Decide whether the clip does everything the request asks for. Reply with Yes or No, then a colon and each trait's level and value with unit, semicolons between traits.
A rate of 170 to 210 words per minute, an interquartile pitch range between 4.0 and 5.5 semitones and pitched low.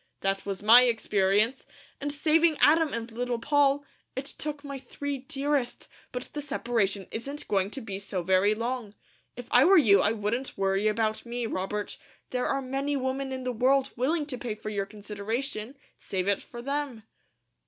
No: average, 175 wpm; average, 4.8 semitones; high, 245 Hz